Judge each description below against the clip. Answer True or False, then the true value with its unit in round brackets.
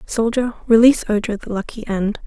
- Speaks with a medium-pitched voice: False (220 Hz)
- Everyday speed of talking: True (160 wpm)